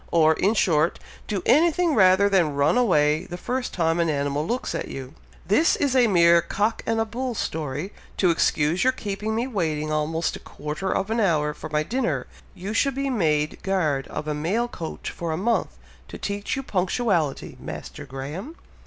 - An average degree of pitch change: No, wide, 6.7 semitones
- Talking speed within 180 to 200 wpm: Yes, average, 190 wpm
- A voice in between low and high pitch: Yes, medium, 180 Hz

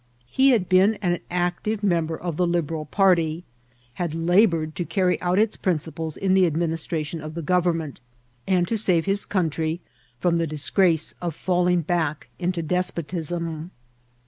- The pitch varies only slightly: Yes, narrow, 2.2 semitones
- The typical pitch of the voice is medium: Yes, medium, 175 Hz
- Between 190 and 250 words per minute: No, average, 180 wpm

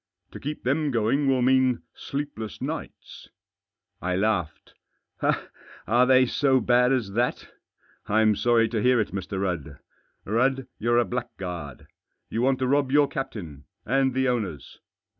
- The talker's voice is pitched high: No, low, 120 Hz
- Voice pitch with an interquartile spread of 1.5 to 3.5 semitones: No, average, 4.3 semitones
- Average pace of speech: Yes, average, 150 wpm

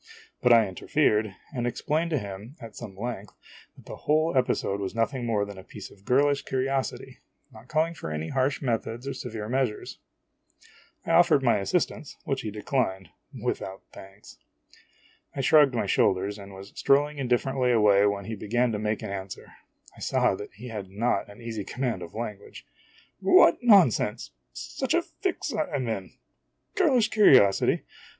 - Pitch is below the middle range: Yes, low, 115 Hz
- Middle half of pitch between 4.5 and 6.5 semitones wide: Yes, average, 5.0 semitones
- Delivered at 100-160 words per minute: No, average, 170 wpm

